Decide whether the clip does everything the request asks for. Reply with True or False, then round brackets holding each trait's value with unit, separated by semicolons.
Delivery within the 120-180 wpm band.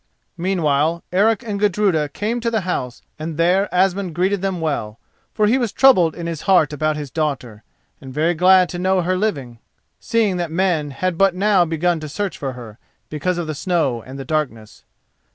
False (190 wpm)